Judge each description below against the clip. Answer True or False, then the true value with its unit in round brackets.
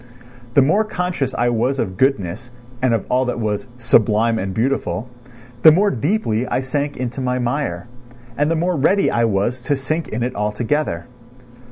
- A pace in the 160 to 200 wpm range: True (175 wpm)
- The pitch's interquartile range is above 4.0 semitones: True (4.4 semitones)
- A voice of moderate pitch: False (125 Hz)